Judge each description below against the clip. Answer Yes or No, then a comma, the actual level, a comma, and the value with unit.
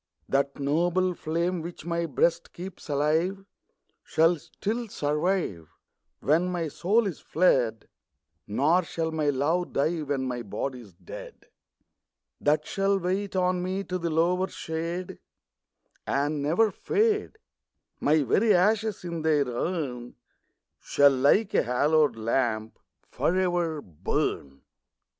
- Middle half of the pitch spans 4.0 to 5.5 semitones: Yes, average, 4.4 semitones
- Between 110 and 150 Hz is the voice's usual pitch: No, medium, 160 Hz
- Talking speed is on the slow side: Yes, slow, 120 wpm